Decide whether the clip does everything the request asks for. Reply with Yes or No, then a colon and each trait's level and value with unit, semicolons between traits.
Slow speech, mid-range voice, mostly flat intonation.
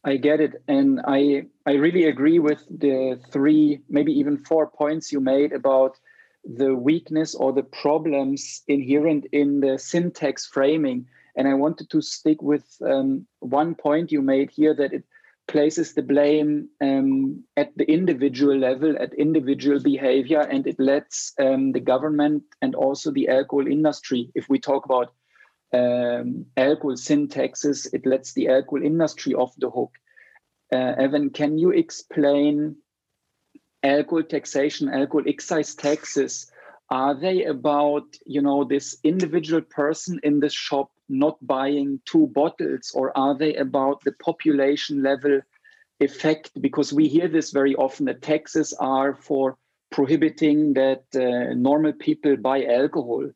No: average, 145 wpm; medium, 145 Hz; narrow, 2.3 semitones